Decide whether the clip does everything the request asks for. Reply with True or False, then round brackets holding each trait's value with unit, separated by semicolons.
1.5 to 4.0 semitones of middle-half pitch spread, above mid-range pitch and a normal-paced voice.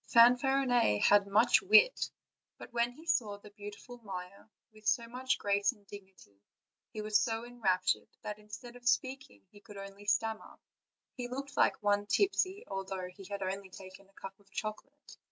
True (3.6 semitones; 210 Hz; 175 wpm)